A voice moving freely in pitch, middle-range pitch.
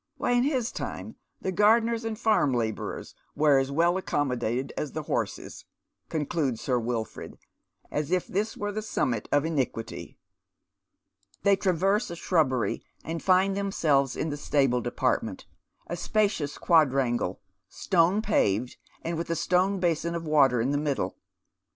Yes: wide, 6.2 semitones; medium, 160 Hz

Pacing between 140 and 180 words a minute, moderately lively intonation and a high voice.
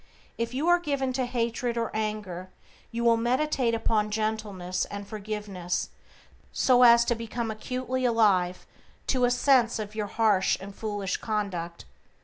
Yes: average, 145 wpm; average, 3.0 semitones; high, 225 Hz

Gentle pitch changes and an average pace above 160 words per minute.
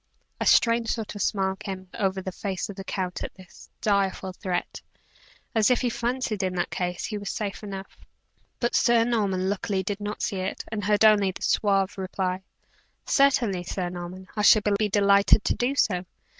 Yes: narrow, 2.3 semitones; average, 185 wpm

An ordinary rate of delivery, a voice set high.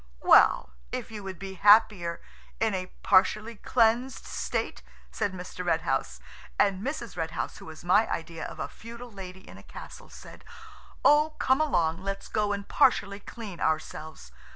Yes: average, 165 wpm; high, 195 Hz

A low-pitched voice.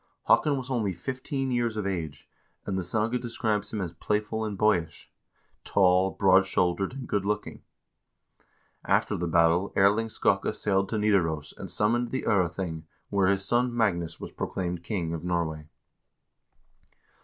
Yes: low, 100 Hz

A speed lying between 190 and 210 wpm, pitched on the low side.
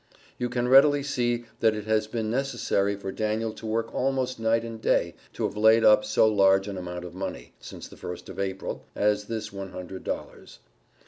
Yes: average, 200 wpm; low, 110 Hz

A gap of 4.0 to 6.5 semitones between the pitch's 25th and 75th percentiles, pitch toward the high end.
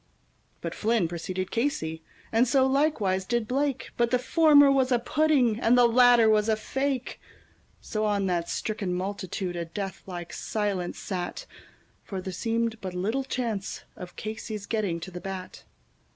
Yes: average, 4.8 semitones; high, 215 Hz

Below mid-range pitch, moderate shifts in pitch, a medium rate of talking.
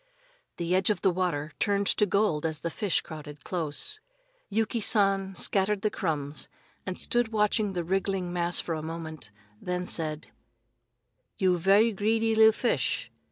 No: medium, 185 Hz; average, 4.2 semitones; average, 155 wpm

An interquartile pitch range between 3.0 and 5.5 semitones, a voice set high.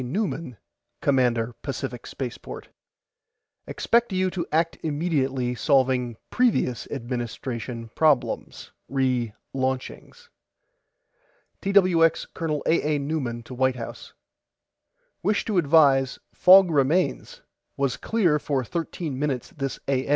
No: average, 4.7 semitones; medium, 140 Hz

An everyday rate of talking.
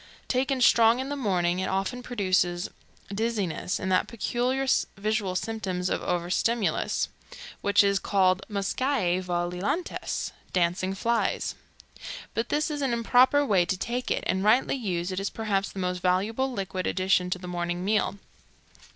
Yes: average, 150 wpm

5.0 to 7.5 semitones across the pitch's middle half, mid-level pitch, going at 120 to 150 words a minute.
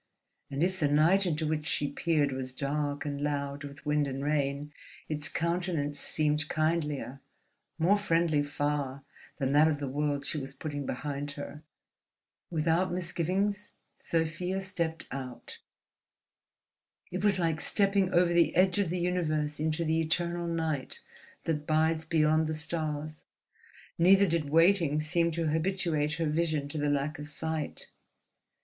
No: narrow, 2.6 semitones; medium, 155 Hz; average, 145 wpm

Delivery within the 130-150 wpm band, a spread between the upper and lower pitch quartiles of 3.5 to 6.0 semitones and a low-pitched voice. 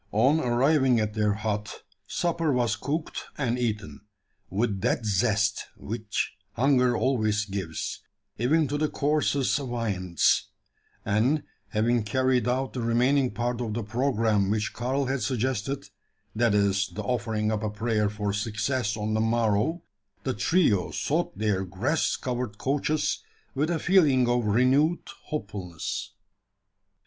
Yes: slow, 135 wpm; average, 3.9 semitones; low, 120 Hz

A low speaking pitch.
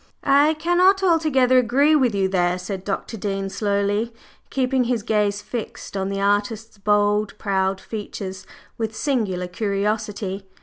No: high, 210 Hz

